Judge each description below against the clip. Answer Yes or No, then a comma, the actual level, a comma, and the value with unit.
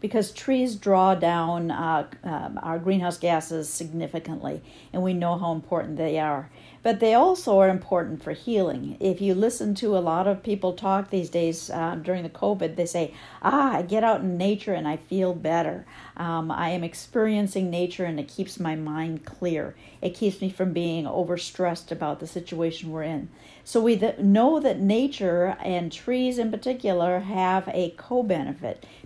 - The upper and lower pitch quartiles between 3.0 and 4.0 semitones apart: Yes, average, 3.3 semitones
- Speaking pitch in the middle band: Yes, medium, 180 Hz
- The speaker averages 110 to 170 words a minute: No, average, 180 wpm